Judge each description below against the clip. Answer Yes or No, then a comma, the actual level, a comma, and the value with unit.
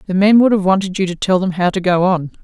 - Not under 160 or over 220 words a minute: No, fast, 320 wpm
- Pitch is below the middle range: No, medium, 185 Hz